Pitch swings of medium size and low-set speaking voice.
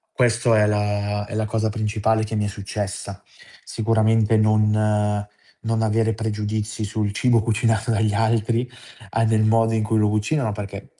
No: narrow, 1.3 semitones; low, 110 Hz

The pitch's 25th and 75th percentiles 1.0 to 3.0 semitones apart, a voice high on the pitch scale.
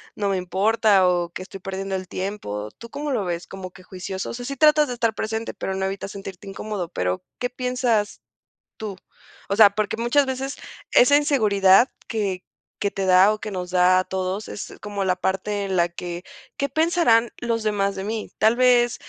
No: average, 3.7 semitones; high, 200 Hz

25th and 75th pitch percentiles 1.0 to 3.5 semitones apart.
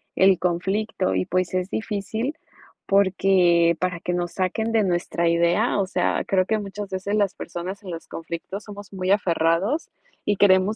Yes: average, 2.7 semitones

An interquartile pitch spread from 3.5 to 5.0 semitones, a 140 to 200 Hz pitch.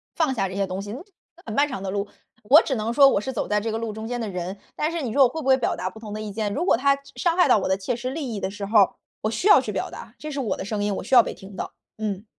No: average, 4.7 semitones; high, 220 Hz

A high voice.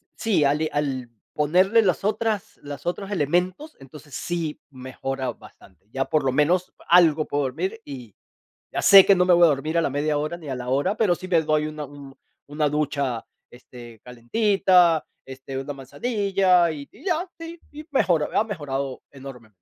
No: medium, 150 Hz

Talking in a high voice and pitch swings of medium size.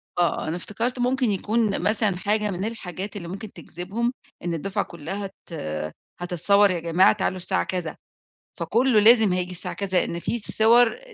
Yes: high, 200 Hz; average, 3.8 semitones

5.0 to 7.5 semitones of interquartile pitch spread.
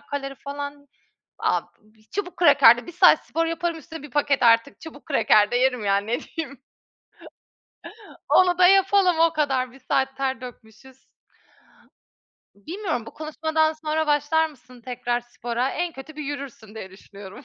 No: average, 4.5 semitones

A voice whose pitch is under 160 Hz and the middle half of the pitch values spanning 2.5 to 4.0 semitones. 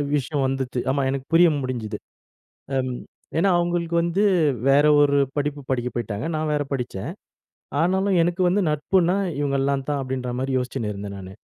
No: medium, 140 Hz; average, 4.8 semitones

